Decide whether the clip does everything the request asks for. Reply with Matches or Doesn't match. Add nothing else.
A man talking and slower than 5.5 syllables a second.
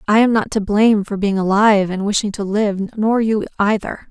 Doesn't match